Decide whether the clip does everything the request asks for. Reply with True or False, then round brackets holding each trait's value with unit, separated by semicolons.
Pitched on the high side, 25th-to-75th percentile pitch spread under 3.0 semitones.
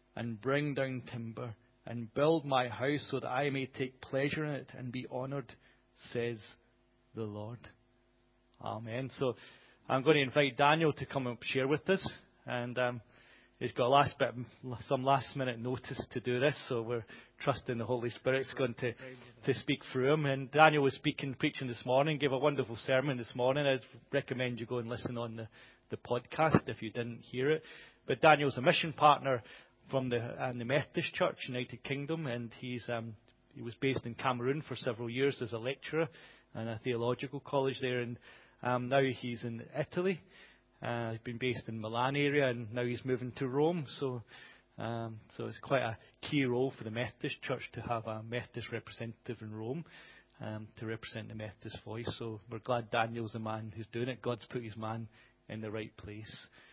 False (125 Hz; 2.5 semitones)